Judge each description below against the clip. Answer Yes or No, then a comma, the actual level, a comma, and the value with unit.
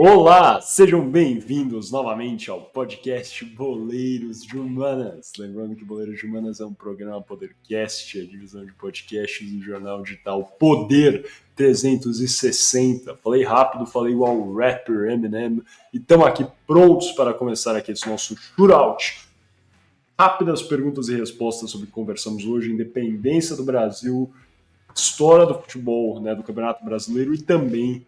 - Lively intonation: No, average, 3.7 semitones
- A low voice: Yes, low, 115 Hz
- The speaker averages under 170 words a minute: Yes, average, 140 wpm